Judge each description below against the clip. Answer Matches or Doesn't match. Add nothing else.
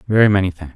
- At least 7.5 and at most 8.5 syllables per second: Matches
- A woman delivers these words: Doesn't match